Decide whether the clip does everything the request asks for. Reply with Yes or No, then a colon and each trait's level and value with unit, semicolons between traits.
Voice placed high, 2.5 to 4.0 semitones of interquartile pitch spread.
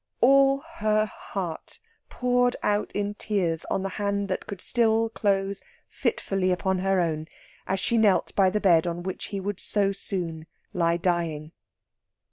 Yes: high, 195 Hz; average, 3.1 semitones